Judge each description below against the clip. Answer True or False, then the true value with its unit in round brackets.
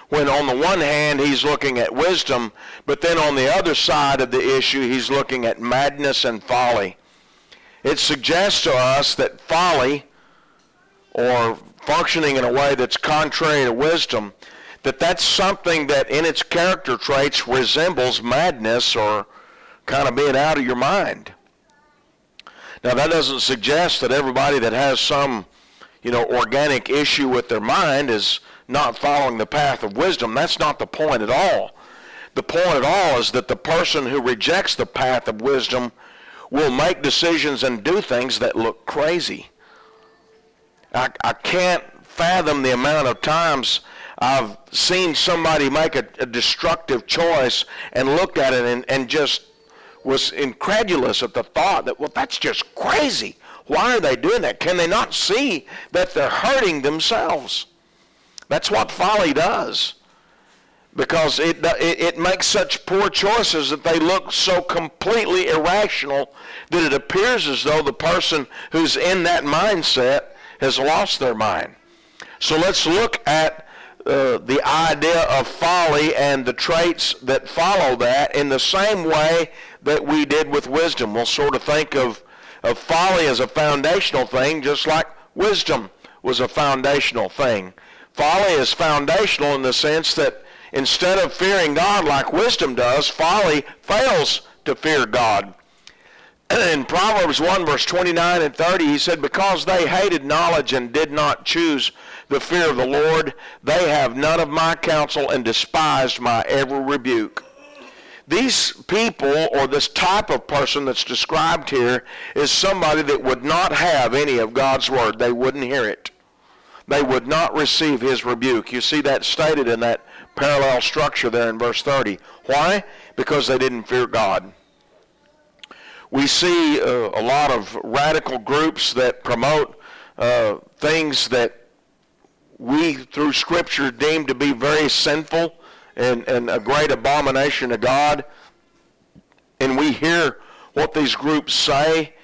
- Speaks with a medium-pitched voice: True (150 Hz)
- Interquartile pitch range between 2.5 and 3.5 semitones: False (4.3 semitones)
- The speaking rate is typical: True (155 wpm)